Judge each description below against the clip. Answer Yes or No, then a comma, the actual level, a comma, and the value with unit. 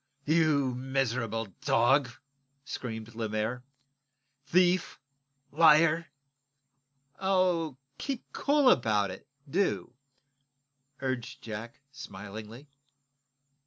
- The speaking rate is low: Yes, slow, 85 wpm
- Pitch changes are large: Yes, wide, 6.4 semitones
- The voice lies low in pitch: Yes, low, 130 Hz